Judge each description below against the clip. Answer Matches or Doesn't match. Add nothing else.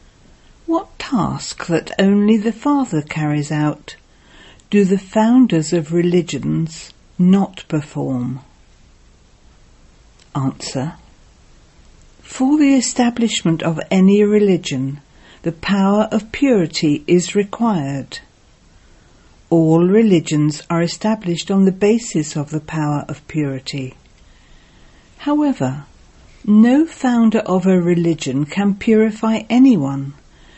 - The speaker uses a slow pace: Matches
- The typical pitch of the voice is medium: Matches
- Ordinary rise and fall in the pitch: Doesn't match